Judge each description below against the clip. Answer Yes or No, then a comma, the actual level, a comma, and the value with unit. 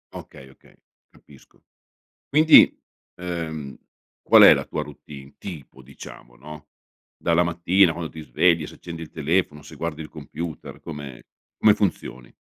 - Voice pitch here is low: Yes, very low, 80 Hz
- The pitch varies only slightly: No, average, 3.1 semitones